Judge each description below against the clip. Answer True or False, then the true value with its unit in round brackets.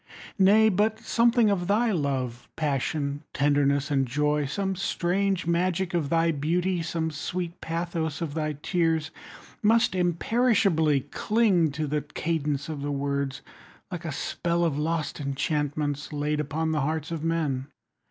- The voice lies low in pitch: False (160 Hz)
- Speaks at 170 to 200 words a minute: False (150 wpm)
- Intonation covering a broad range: False (3.5 semitones)